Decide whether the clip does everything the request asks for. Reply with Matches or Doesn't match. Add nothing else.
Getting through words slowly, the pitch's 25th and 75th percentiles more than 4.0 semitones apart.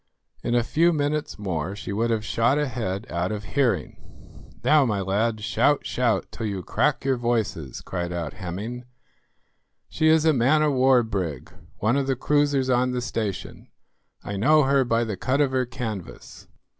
Doesn't match